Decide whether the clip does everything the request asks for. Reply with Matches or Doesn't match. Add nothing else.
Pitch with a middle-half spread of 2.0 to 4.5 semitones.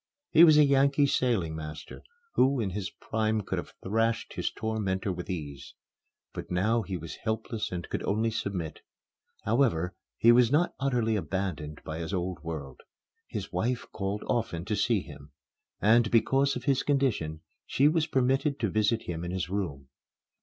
Doesn't match